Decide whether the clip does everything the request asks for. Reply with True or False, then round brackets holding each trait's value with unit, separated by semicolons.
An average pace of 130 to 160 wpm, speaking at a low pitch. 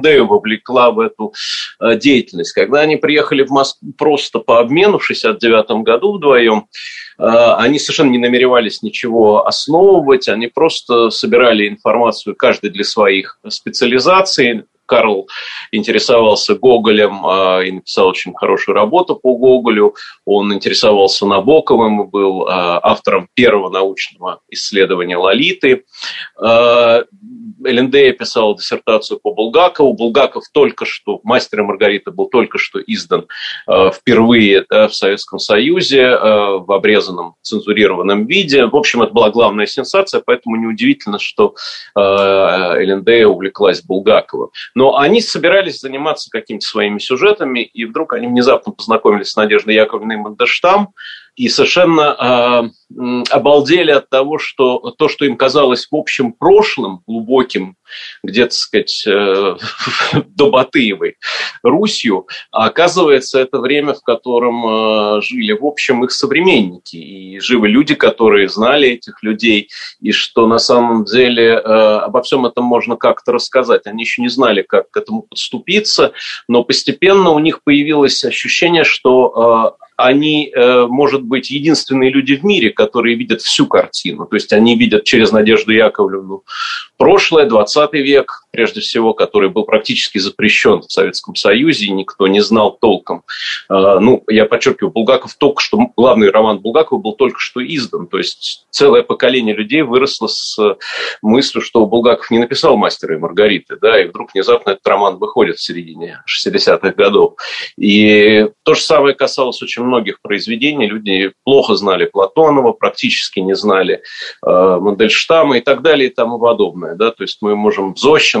True (140 wpm; 125 Hz)